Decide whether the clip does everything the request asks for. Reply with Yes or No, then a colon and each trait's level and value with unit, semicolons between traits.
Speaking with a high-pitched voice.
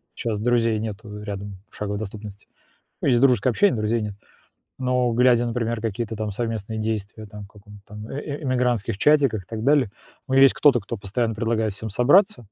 No: low, 110 Hz